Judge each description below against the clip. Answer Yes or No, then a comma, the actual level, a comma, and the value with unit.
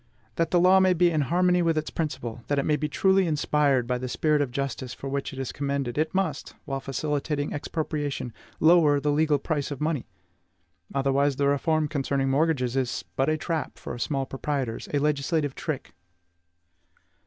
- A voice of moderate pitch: Yes, medium, 145 Hz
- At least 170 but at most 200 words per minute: Yes, average, 185 wpm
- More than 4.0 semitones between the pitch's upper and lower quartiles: No, narrow, 2.5 semitones